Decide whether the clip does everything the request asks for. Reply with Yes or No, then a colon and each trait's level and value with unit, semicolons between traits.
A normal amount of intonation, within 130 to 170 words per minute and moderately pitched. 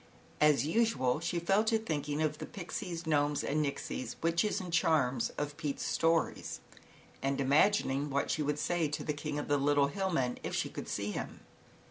No: average, 3.2 semitones; average, 185 wpm; medium, 150 Hz